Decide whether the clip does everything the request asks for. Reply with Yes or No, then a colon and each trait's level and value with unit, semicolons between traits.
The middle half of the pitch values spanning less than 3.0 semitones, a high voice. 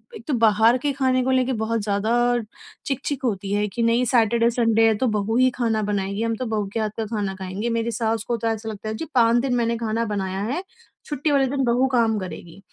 Yes: narrow, 2.5 semitones; high, 230 Hz